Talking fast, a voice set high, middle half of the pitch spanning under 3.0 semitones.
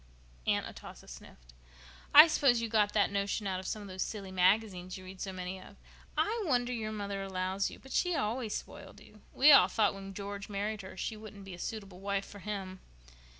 Yes: fast, 210 wpm; high, 200 Hz; narrow, 2.5 semitones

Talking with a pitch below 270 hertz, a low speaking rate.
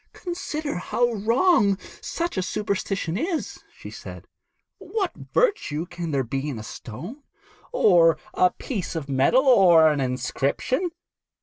Yes: high, 190 Hz; slow, 130 wpm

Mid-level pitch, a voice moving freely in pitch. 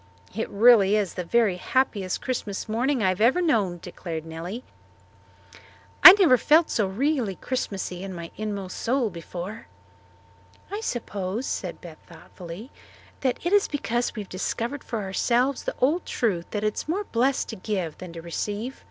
No: high, 215 Hz; wide, 5.7 semitones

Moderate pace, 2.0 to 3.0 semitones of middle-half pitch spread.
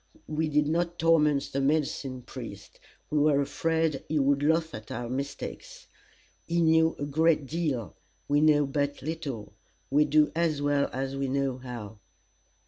Yes: average, 155 wpm; average, 2.7 semitones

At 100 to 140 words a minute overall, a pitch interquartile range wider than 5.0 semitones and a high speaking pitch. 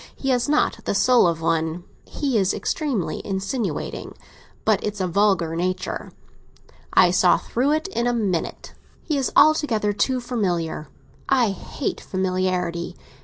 Yes: slow, 135 wpm; wide, 5.6 semitones; high, 205 Hz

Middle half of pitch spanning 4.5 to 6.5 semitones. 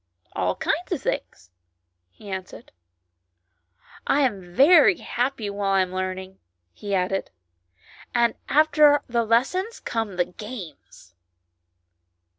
Yes: wide, 5.6 semitones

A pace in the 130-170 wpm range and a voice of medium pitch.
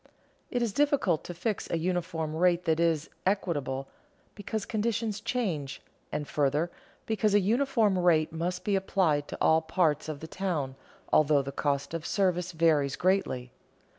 Yes: average, 155 wpm; medium, 170 Hz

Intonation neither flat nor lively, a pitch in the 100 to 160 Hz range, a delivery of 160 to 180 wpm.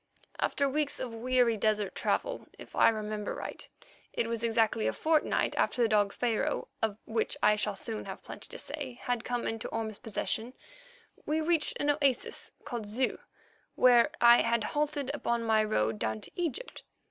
No: average, 4.6 semitones; high, 235 Hz; average, 165 wpm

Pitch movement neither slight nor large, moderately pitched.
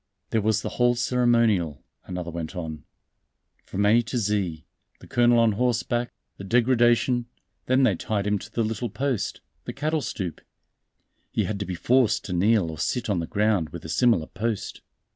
No: average, 4.5 semitones; low, 110 Hz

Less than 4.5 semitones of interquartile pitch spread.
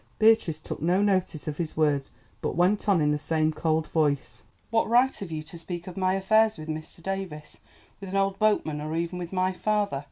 Yes: average, 4.0 semitones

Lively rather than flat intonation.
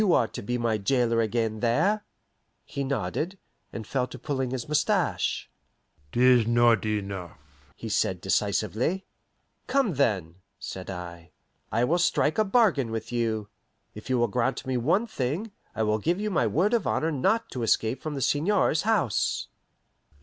Yes: wide, 6.5 semitones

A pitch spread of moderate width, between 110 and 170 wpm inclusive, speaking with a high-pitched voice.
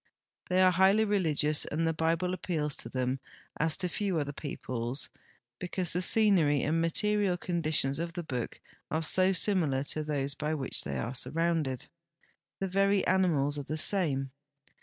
No: average, 4.3 semitones; average, 160 wpm; medium, 160 Hz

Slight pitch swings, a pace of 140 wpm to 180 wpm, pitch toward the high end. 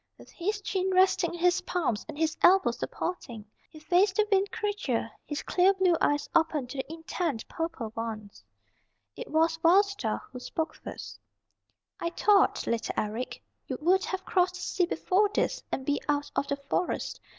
No: average, 4.8 semitones; average, 175 wpm; very high, 340 Hz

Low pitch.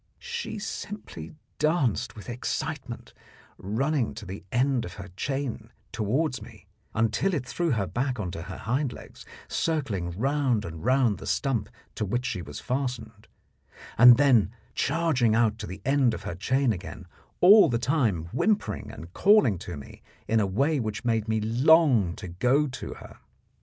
Yes: low, 120 Hz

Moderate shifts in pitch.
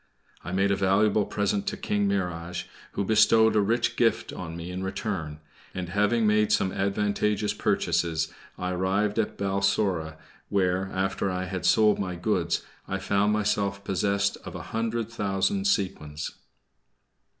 No: narrow, 2.3 semitones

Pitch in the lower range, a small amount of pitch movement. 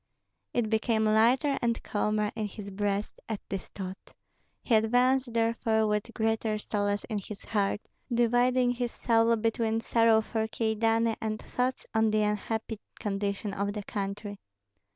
No: high, 220 Hz; narrow, 1.8 semitones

